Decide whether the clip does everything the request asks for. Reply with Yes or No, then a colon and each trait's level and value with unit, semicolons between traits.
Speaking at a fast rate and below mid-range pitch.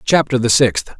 No: average, 180 wpm; low, 125 Hz